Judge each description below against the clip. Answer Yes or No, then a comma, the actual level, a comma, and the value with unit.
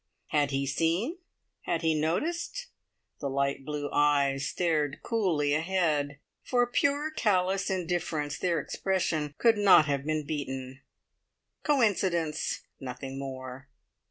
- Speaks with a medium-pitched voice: Yes, medium, 155 Hz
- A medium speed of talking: No, slow, 115 wpm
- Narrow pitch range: No, average, 5.1 semitones